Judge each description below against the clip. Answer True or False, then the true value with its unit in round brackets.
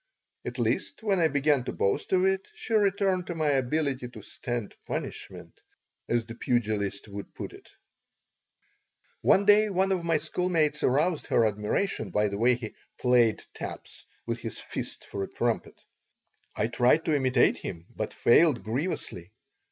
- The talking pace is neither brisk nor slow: True (160 wpm)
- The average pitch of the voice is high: False (135 Hz)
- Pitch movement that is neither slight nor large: False (7.6 semitones)